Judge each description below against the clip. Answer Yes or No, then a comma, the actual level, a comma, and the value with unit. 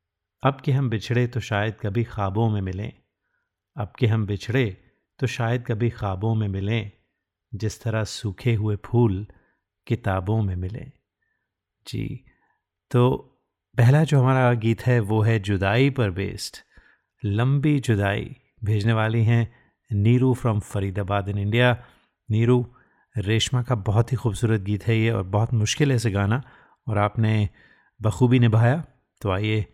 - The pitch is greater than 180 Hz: No, low, 115 Hz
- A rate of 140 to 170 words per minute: Yes, average, 145 wpm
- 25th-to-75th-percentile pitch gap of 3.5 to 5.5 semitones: No, average, 3.0 semitones